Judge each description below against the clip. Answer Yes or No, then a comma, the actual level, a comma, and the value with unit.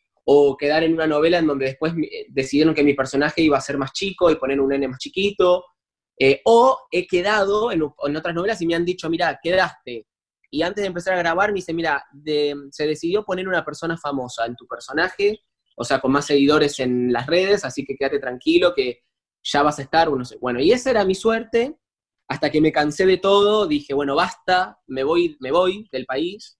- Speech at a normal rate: No, fast, 215 wpm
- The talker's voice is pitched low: No, medium, 155 Hz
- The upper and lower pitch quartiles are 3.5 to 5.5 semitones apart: Yes, average, 4.8 semitones